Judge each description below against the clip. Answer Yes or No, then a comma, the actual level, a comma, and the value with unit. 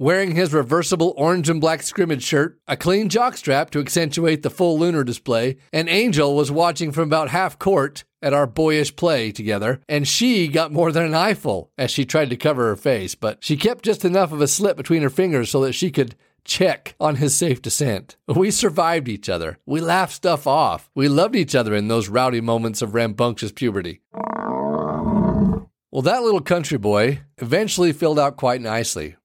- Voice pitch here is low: No, medium, 150 Hz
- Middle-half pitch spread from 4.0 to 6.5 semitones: Yes, average, 5.2 semitones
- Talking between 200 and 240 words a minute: No, average, 190 wpm